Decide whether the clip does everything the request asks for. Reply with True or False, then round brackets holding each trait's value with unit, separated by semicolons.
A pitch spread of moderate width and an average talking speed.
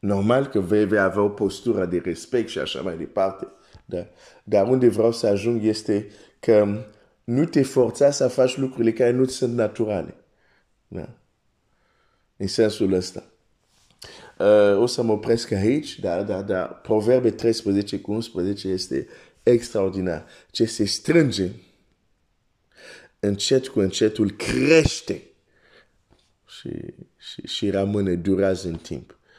True (3.3 semitones; 130 wpm)